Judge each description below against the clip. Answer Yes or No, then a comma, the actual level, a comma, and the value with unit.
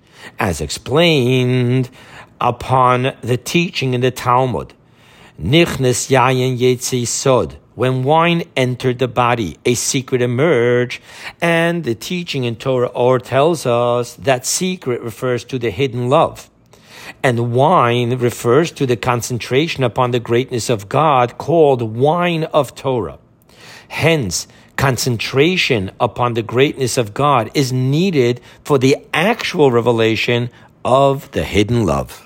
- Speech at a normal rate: No, slow, 125 wpm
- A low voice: Yes, low, 125 Hz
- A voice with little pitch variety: Yes, narrow, 2.3 semitones